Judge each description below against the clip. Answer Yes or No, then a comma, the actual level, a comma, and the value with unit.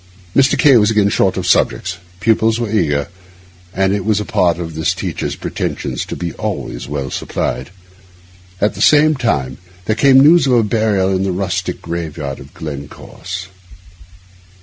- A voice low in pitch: Yes, very low, 95 Hz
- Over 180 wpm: No, average, 170 wpm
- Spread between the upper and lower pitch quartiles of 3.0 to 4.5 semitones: No, average, 5.3 semitones